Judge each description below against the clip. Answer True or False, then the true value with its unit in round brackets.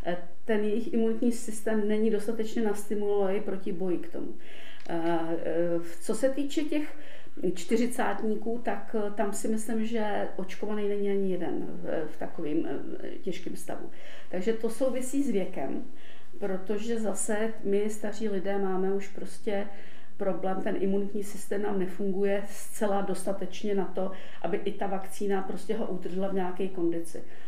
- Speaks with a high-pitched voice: True (205 Hz)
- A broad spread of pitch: False (2.6 semitones)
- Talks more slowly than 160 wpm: True (135 wpm)